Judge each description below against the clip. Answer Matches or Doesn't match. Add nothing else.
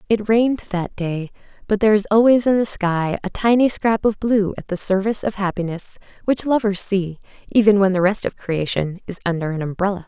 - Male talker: Doesn't match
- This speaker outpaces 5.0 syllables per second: Matches